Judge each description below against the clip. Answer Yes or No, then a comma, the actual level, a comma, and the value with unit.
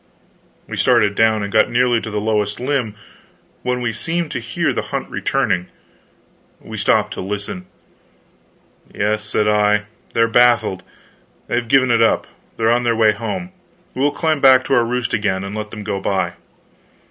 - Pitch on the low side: Yes, low, 115 Hz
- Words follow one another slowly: No, average, 170 wpm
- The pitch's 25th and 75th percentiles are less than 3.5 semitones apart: Yes, average, 2.9 semitones